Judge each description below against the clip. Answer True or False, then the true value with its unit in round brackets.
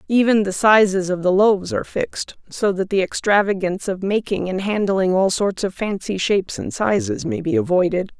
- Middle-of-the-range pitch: False (195 Hz)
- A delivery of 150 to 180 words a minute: False (190 wpm)